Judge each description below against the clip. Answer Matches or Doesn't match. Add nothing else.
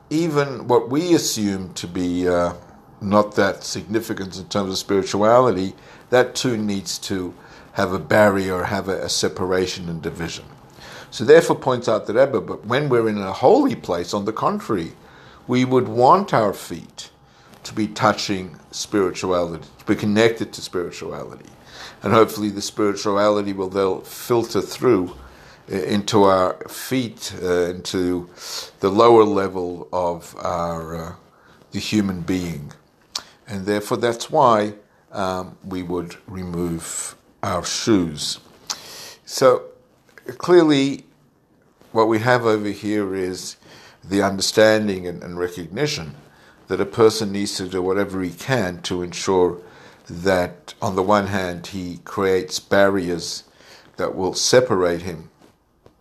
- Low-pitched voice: Matches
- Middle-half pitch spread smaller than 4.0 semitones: Matches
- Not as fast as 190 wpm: Matches